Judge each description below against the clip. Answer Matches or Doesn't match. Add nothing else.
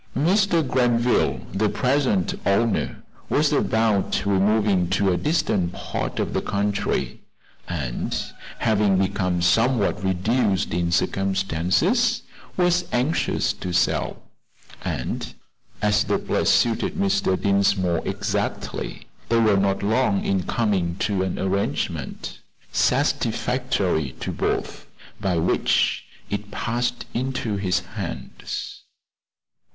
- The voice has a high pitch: Doesn't match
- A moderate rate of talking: Doesn't match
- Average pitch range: Matches